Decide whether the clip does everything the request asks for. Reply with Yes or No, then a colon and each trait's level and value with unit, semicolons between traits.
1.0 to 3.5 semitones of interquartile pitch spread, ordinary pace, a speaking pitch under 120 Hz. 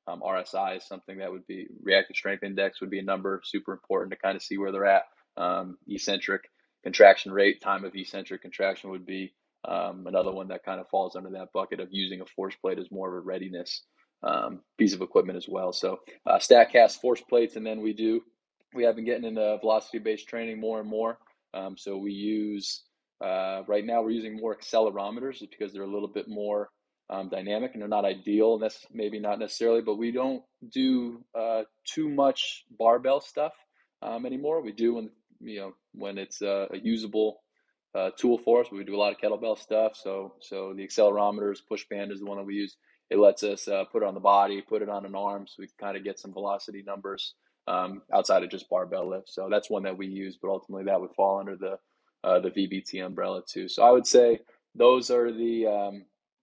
No: average, 2.7 semitones; fast, 220 wpm; low, 105 Hz